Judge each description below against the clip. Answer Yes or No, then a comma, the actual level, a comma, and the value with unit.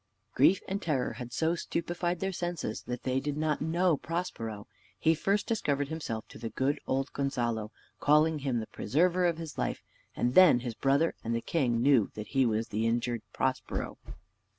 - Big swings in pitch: Yes, wide, 5.7 semitones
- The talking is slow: No, average, 180 wpm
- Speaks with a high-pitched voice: No, medium, 140 Hz